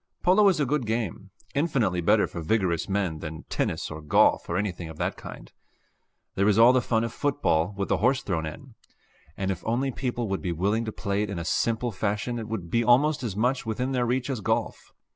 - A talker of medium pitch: No, low, 110 Hz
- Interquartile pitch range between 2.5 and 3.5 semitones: No, average, 4.7 semitones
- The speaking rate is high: Yes, fast, 220 wpm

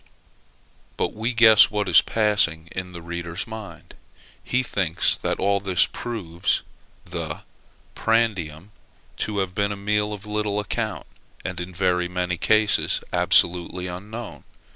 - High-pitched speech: No, low, 100 Hz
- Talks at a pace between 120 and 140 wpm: Yes, slow, 135 wpm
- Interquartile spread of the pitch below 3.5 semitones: Yes, average, 3.1 semitones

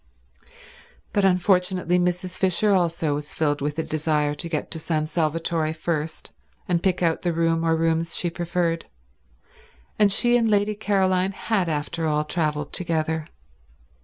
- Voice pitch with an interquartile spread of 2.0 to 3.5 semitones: Yes, average, 2.7 semitones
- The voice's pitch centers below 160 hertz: No, medium, 165 Hz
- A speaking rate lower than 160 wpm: Yes, average, 150 wpm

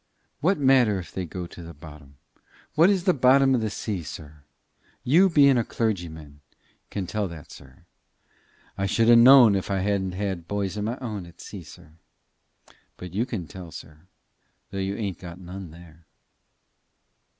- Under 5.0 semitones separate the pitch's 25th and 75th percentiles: No, wide, 5.5 semitones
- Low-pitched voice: Yes, very low, 95 Hz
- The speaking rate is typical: Yes, average, 175 wpm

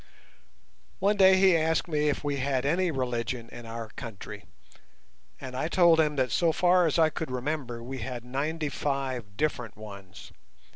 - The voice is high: No, medium, 140 Hz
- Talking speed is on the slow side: No, average, 165 wpm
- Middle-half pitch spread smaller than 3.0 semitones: No, average, 4.8 semitones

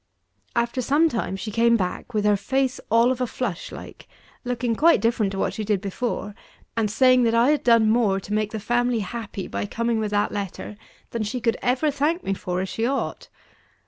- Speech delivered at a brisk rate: Yes, fast, 210 wpm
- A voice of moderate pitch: No, high, 230 Hz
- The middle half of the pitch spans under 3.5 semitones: Yes, average, 3.1 semitones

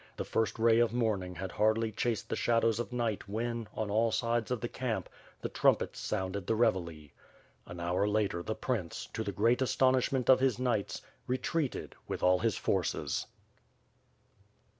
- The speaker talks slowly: No, average, 165 wpm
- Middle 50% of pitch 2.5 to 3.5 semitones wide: Yes, average, 3.2 semitones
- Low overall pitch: Yes, low, 115 Hz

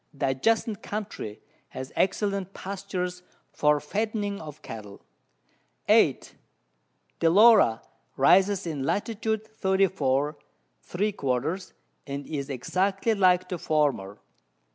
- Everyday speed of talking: No, slow, 100 wpm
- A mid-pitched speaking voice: Yes, medium, 180 Hz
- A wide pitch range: Yes, wide, 6.2 semitones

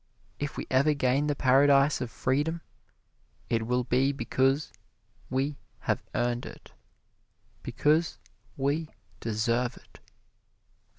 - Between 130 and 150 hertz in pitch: Yes, low, 135 Hz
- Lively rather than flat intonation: No, average, 2.7 semitones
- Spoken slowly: Yes, slow, 110 wpm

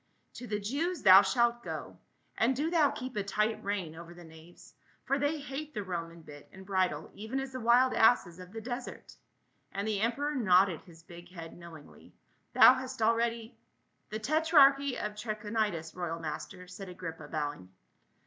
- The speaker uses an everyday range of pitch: No, wide, 6.5 semitones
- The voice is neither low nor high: No, high, 210 Hz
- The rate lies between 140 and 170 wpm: No, average, 185 wpm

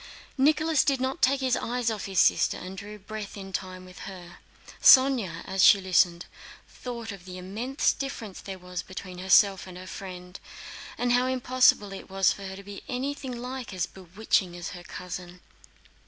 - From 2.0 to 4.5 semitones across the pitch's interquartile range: No, average, 5.2 semitones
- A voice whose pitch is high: Yes, high, 195 Hz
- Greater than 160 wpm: Yes, average, 180 wpm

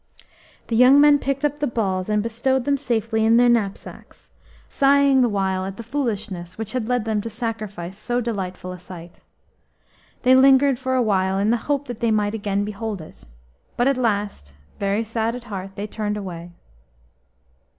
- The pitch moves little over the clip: No, average, 3.9 semitones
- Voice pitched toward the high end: Yes, high, 220 Hz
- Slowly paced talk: No, average, 180 wpm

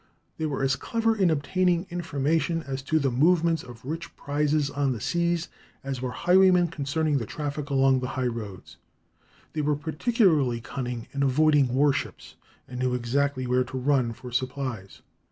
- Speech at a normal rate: Yes, average, 165 wpm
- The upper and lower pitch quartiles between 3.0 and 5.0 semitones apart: Yes, average, 3.9 semitones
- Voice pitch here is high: No, medium, 140 Hz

